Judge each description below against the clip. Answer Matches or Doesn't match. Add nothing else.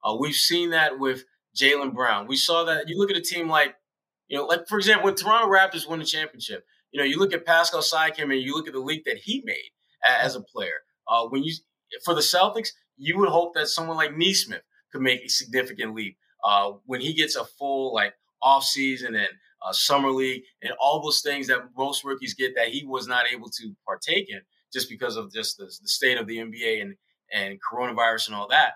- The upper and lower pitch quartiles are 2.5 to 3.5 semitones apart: Doesn't match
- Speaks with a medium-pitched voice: Matches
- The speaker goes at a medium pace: Doesn't match